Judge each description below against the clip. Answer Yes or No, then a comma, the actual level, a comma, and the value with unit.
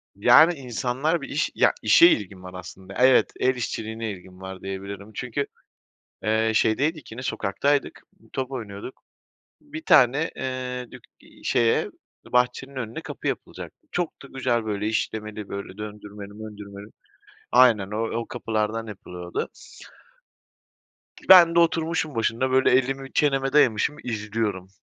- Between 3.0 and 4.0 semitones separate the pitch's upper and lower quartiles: No, average, 4.4 semitones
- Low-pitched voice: Yes, low, 115 Hz